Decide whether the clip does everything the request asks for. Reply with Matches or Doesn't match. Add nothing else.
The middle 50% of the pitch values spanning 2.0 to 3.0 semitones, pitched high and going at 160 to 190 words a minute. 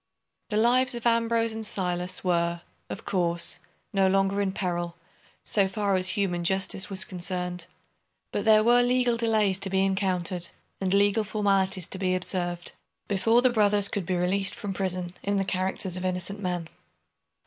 Matches